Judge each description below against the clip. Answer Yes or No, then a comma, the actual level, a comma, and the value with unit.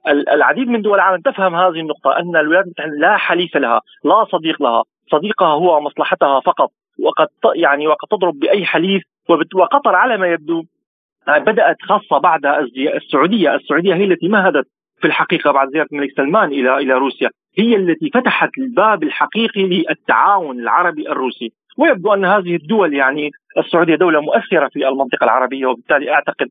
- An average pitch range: No, wide, 5.8 semitones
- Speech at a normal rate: No, fast, 155 wpm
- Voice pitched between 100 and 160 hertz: No, medium, 170 Hz